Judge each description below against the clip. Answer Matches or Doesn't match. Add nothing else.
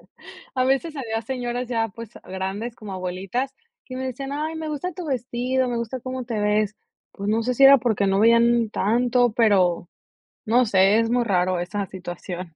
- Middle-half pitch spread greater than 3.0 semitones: Matches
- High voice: Matches